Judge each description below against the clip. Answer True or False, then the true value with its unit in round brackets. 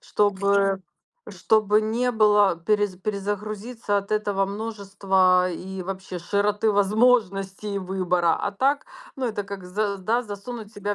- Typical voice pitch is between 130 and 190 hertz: False (205 Hz)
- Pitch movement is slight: True (1.8 semitones)